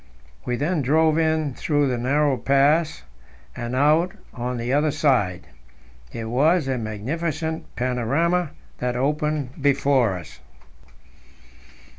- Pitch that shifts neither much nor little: Yes, average, 3.9 semitones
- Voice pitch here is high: No, medium, 140 Hz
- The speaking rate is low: Yes, slow, 115 wpm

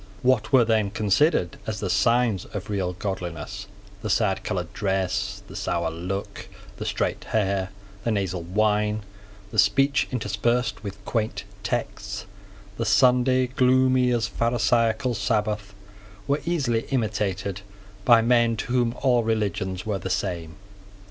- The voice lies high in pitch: No, low, 105 Hz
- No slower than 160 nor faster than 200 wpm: No, slow, 135 wpm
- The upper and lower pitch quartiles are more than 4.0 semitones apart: No, average, 3.6 semitones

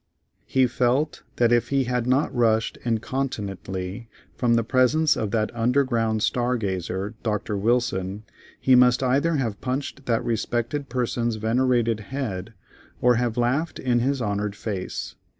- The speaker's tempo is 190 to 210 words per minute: No, average, 140 wpm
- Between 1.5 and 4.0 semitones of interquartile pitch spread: Yes, average, 2.7 semitones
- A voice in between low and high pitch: No, low, 120 Hz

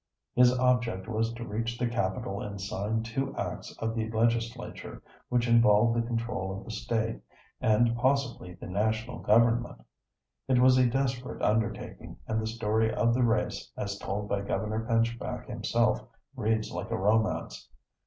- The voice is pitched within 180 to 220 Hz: No, low, 115 Hz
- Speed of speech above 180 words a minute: No, average, 155 wpm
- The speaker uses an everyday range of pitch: No, narrow, 1.9 semitones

